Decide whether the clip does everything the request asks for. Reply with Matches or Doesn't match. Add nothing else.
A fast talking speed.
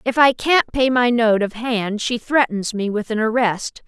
Matches